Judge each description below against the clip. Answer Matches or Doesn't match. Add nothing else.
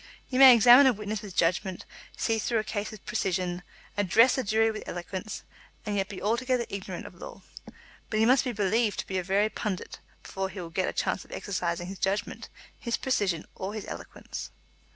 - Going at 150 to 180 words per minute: Doesn't match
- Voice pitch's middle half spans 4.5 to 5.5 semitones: Doesn't match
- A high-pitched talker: Matches